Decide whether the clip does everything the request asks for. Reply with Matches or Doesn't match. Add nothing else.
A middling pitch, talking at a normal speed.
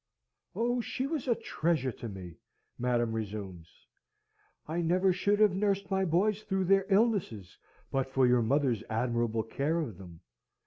Matches